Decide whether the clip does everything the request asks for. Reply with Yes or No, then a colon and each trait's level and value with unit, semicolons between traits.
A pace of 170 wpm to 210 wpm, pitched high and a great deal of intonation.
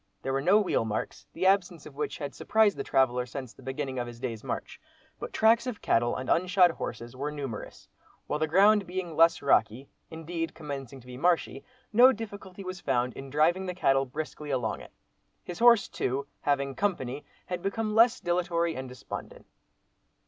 No: average, 185 wpm; medium, 155 Hz; wide, 5.9 semitones